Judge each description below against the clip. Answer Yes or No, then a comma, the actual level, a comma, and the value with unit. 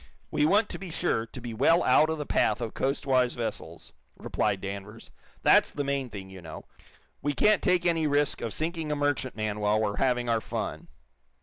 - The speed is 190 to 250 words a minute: Yes, average, 195 wpm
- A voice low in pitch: Yes, low, 130 Hz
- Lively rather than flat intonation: Yes, wide, 5.7 semitones